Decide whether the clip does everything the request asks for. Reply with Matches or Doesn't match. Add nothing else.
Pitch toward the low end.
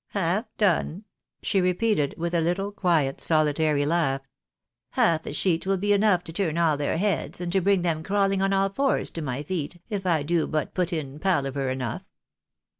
Doesn't match